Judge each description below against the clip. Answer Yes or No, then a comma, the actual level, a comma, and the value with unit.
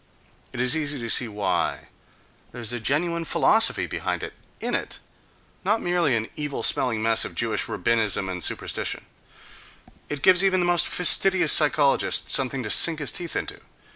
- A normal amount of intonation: No, wide, 7.0 semitones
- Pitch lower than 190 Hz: Yes, medium, 140 Hz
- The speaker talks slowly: No, average, 165 wpm